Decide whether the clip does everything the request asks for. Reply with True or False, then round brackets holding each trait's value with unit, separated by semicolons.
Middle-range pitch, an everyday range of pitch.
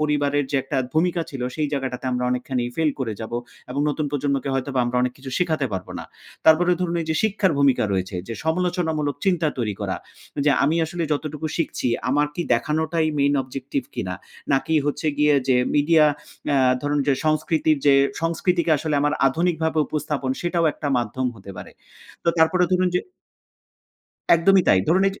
True (150 Hz; 3.5 semitones)